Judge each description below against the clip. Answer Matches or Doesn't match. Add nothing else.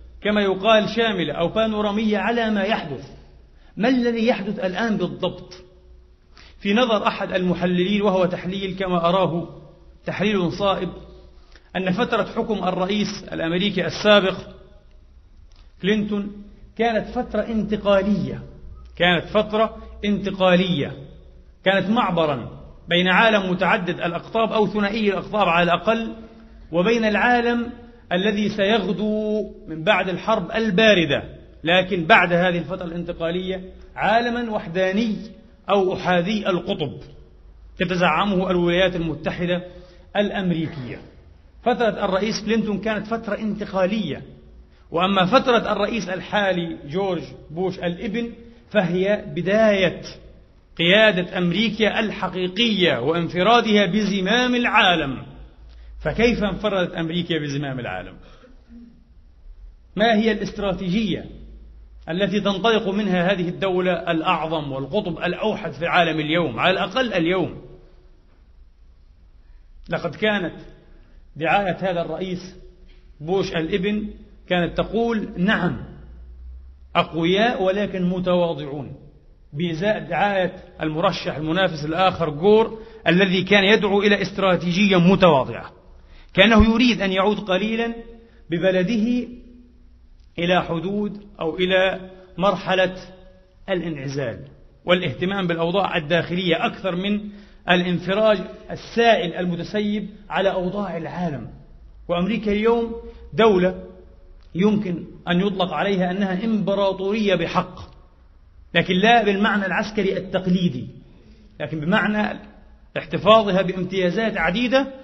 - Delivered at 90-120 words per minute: Matches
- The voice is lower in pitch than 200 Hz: Matches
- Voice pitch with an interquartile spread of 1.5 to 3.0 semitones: Doesn't match